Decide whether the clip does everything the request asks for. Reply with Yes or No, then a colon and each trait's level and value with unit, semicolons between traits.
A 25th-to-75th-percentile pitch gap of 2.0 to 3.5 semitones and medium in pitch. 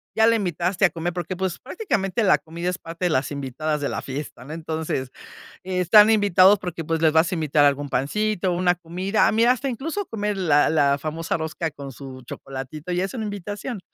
No: average, 4.7 semitones; medium, 175 Hz